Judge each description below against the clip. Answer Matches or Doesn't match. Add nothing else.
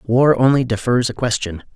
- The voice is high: Doesn't match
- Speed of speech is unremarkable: Matches